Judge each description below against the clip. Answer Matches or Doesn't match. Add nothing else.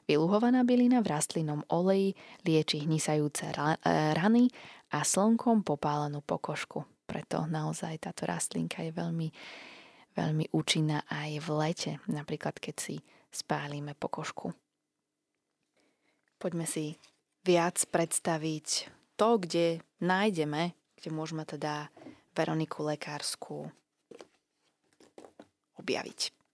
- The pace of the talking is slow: Matches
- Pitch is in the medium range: Matches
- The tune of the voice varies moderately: Matches